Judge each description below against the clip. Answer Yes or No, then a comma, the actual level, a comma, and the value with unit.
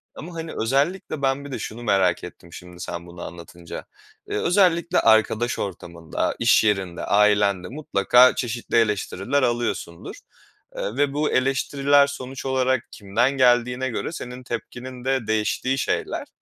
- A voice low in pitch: Yes, low, 120 Hz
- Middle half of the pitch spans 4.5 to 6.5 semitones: Yes, average, 5.0 semitones